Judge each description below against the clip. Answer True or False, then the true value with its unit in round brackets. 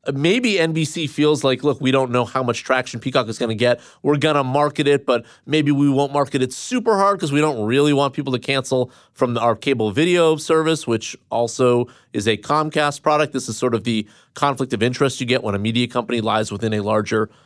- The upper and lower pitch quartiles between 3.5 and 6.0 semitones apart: True (3.8 semitones)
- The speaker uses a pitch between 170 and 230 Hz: False (130 Hz)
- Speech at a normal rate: False (225 wpm)